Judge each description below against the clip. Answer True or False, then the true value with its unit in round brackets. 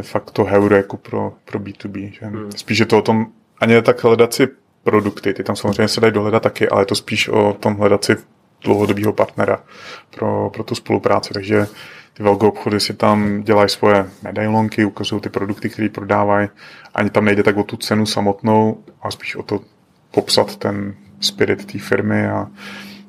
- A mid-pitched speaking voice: False (105 Hz)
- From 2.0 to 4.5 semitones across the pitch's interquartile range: False (1.2 semitones)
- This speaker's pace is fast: True (185 wpm)